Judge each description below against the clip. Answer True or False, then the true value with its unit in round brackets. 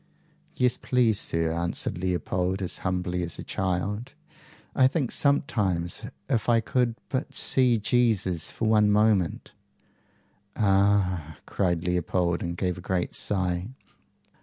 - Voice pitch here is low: True (95 Hz)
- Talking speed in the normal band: False (130 wpm)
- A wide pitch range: False (4.1 semitones)